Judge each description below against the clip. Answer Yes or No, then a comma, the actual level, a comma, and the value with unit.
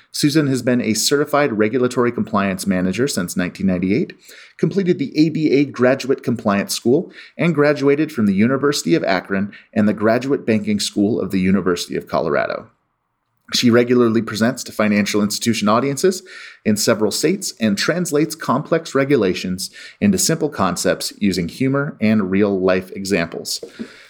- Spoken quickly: No, average, 140 wpm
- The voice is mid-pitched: No, low, 120 Hz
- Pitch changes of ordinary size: No, wide, 6.0 semitones